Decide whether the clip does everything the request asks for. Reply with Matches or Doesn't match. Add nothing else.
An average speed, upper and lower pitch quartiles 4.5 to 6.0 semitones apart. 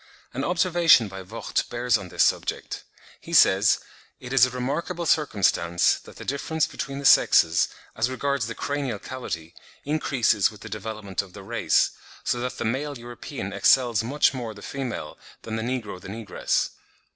Matches